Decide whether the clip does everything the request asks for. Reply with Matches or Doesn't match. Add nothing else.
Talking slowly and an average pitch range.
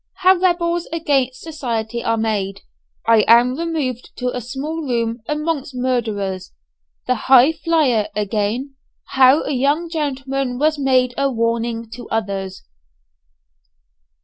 Matches